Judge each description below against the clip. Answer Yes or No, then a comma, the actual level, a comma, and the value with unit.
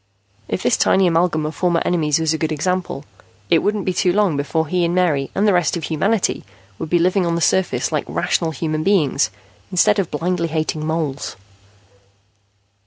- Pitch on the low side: No, medium, 170 Hz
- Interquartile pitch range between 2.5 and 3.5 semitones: Yes, average, 2.8 semitones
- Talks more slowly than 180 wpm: No, average, 185 wpm